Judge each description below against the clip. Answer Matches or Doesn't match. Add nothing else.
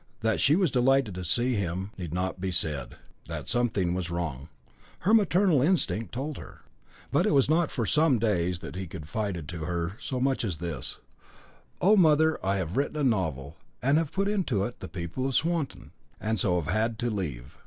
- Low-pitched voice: Matches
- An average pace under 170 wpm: Doesn't match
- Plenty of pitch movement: Matches